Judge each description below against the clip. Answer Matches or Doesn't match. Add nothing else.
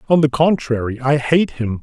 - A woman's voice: Doesn't match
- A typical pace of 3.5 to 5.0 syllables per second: Matches